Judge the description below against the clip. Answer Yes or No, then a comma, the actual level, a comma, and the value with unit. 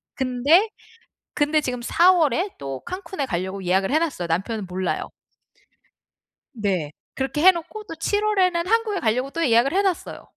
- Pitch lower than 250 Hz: No, very high, 285 Hz